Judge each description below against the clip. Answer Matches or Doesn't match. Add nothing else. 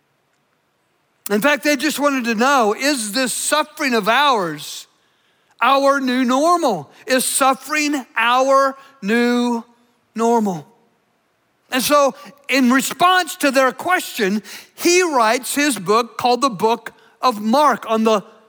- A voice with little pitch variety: Doesn't match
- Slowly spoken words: Matches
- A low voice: Doesn't match